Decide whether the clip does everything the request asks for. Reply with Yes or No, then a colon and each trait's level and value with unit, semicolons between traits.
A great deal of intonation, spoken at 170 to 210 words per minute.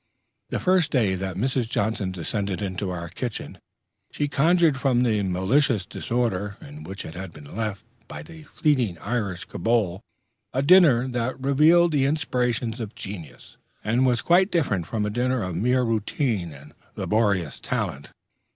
No: wide, 5.8 semitones; average, 155 wpm